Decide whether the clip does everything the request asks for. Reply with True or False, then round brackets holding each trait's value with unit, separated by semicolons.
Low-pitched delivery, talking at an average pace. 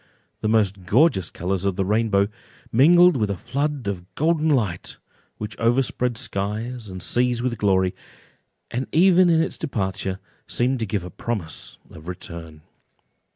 True (110 Hz; 150 wpm)